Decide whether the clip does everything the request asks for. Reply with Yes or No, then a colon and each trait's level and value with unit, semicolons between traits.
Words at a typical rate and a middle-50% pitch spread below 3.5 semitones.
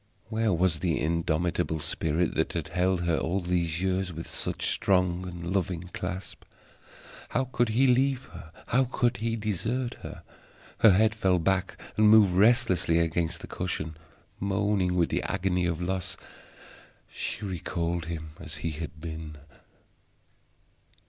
No: average, 145 wpm; average, 3.8 semitones